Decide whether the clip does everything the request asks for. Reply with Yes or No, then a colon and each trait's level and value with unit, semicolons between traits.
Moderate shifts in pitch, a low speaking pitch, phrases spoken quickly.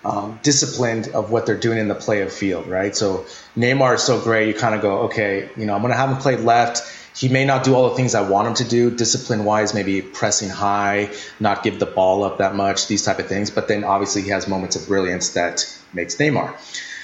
Yes: average, 3.3 semitones; low, 105 Hz; fast, 245 wpm